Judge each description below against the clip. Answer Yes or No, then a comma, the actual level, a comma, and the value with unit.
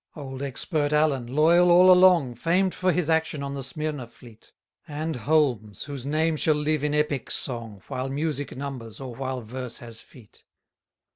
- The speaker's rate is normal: Yes, average, 170 wpm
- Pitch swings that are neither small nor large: Yes, average, 3.7 semitones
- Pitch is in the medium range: Yes, medium, 145 Hz